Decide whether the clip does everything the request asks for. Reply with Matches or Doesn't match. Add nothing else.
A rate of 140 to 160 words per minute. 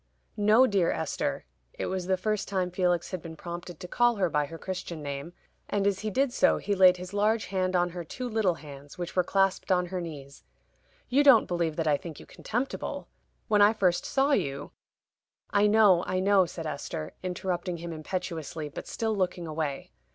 Doesn't match